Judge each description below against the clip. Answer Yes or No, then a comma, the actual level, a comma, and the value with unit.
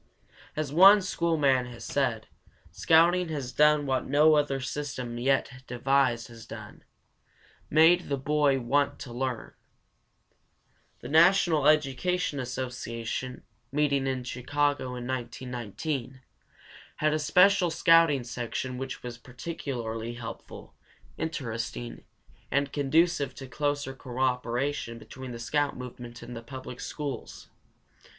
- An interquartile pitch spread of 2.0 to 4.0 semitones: Yes, average, 3.4 semitones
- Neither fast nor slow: No, slow, 115 wpm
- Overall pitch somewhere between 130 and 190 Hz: Yes, low, 135 Hz